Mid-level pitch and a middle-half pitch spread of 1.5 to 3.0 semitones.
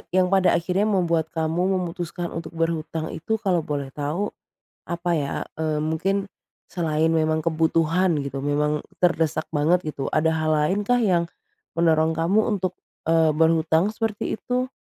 Yes: medium, 165 Hz; narrow, 2.6 semitones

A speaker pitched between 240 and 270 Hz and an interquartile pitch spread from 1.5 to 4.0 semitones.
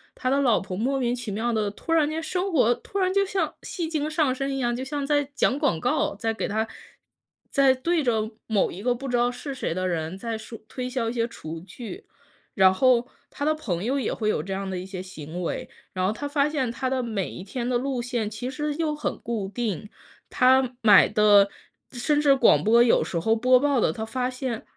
No: high, 245 Hz; average, 4.6 semitones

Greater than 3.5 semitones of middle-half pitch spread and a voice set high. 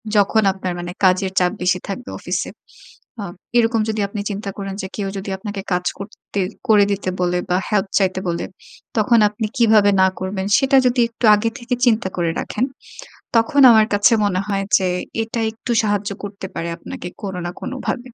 No: average, 2.9 semitones; high, 205 Hz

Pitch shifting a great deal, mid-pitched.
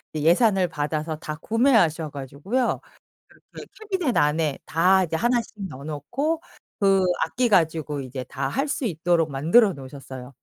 Yes: wide, 7.2 semitones; medium, 165 Hz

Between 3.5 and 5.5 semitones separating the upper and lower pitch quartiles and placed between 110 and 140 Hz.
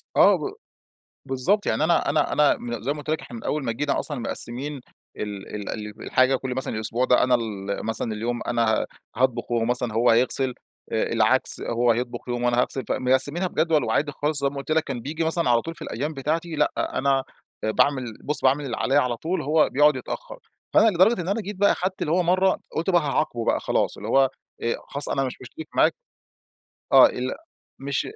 Yes: average, 4.5 semitones; low, 135 Hz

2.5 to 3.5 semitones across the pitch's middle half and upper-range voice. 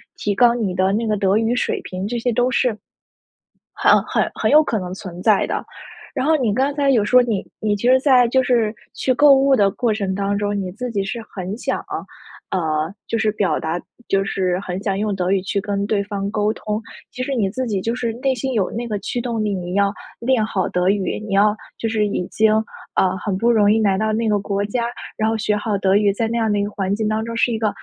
Yes: average, 2.9 semitones; high, 210 Hz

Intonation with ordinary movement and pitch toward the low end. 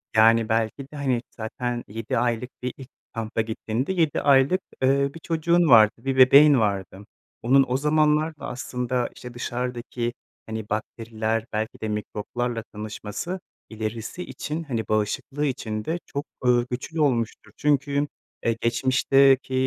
Yes: average, 3.8 semitones; low, 125 Hz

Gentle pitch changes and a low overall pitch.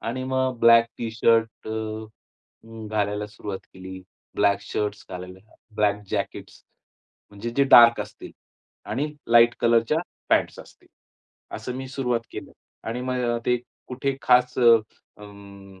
No: average, 3.2 semitones; low, 115 Hz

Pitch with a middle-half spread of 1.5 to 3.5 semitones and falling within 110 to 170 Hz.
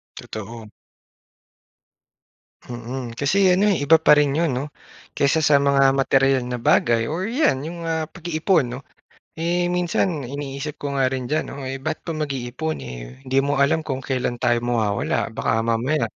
No: average, 4.3 semitones; medium, 140 Hz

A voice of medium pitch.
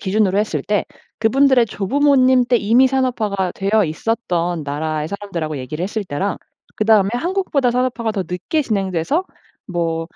No: high, 205 Hz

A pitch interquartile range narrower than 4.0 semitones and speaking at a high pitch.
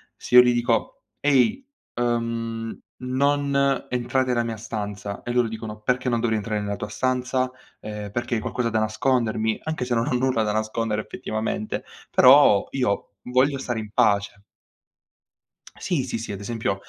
No: average, 2.8 semitones; low, 115 Hz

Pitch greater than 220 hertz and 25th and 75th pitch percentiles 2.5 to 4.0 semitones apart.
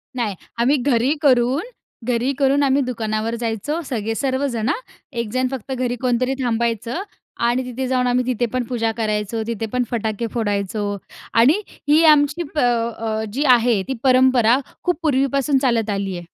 Yes: high, 245 Hz; average, 2.9 semitones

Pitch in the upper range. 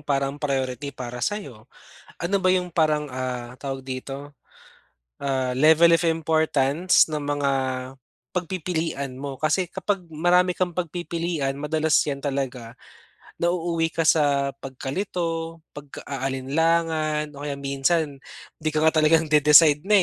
No: medium, 150 Hz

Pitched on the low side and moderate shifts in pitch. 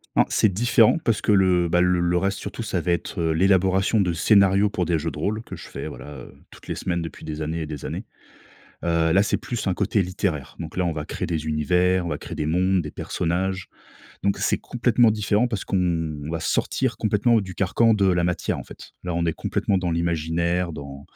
Yes: very low, 90 Hz; average, 3.2 semitones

